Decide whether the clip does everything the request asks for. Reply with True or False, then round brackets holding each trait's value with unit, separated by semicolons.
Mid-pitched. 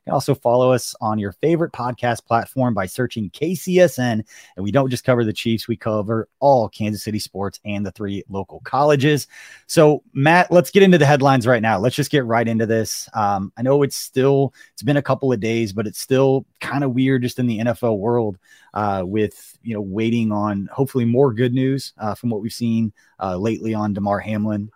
False (115 Hz)